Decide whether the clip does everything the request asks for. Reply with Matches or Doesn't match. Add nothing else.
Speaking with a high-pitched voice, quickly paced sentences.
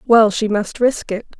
Matches